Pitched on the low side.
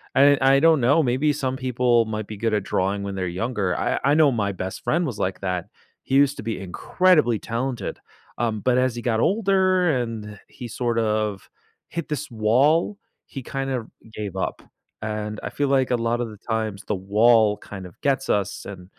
Yes: low, 115 Hz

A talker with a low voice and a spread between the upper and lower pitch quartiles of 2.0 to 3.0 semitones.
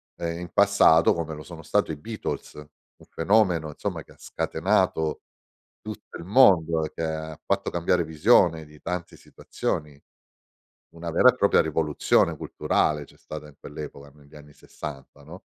Yes: very low, 80 Hz; average, 2.7 semitones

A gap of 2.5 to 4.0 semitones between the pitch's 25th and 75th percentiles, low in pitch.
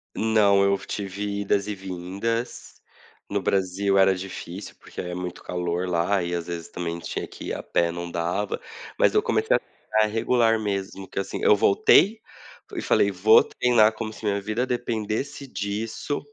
Yes: average, 3.3 semitones; low, 100 Hz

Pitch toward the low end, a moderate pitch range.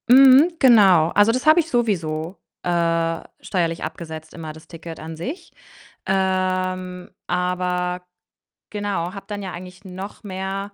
No: medium, 185 Hz; average, 3.3 semitones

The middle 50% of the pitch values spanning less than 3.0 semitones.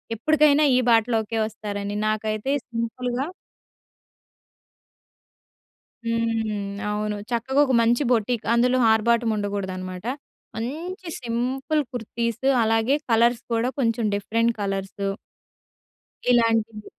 Yes: narrow, 2.4 semitones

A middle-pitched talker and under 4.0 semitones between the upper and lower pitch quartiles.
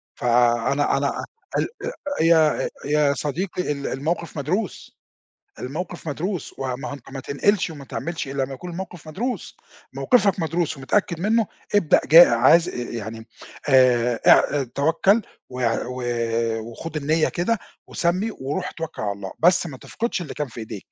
No: medium, 150 Hz; average, 5.1 semitones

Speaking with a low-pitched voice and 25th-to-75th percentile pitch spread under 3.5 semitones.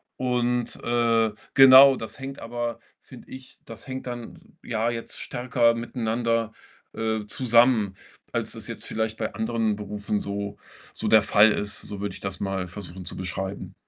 Yes: low, 115 Hz; average, 2.7 semitones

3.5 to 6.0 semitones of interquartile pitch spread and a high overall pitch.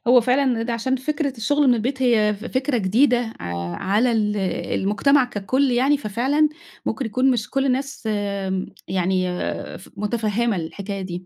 Yes: average, 4.2 semitones; high, 235 Hz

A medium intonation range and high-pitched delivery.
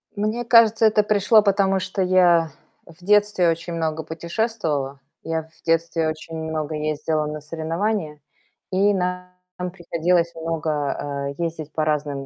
No: average, 3.6 semitones; medium, 165 Hz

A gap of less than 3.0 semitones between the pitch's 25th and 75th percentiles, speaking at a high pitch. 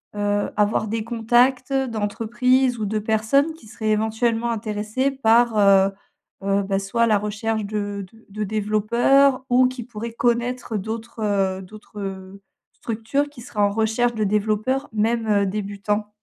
Yes: narrow, 2.5 semitones; high, 220 Hz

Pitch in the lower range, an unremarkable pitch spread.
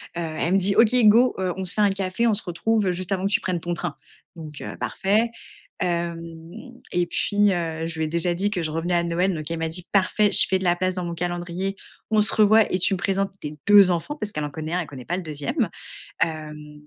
No: medium, 180 Hz; average, 3.0 semitones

